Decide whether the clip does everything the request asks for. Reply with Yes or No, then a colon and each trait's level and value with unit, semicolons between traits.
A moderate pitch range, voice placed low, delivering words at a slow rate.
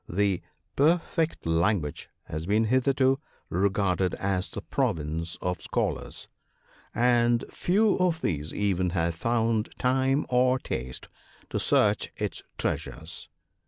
No: wide, 6.8 semitones; low, 105 Hz; slow, 120 wpm